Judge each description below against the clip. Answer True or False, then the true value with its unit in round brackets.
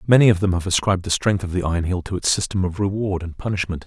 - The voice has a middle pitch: False (95 Hz)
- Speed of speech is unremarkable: False (280 wpm)